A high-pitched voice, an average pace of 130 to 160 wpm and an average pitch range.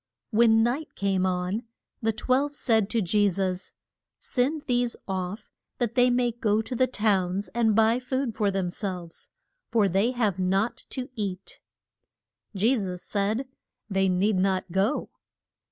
Yes: high, 210 Hz; average, 150 wpm; average, 4.0 semitones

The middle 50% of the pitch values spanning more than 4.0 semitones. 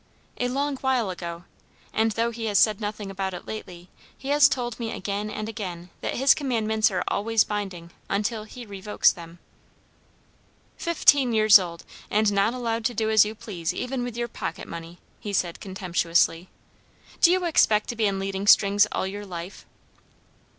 No: average, 3.5 semitones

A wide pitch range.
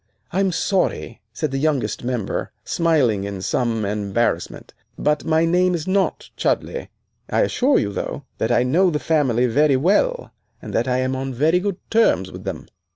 Yes: wide, 6.8 semitones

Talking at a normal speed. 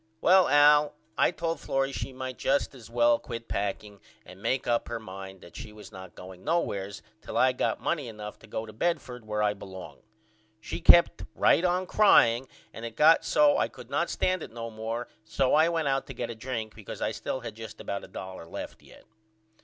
No: fast, 210 wpm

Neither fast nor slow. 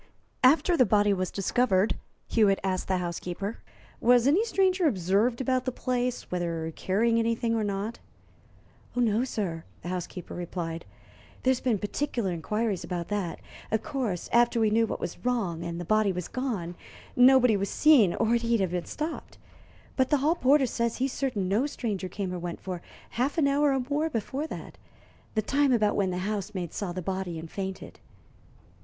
Yes: average, 175 wpm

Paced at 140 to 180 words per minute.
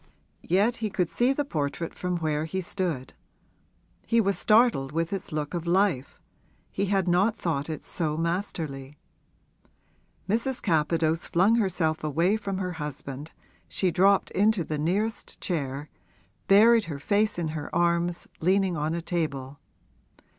Yes: average, 145 wpm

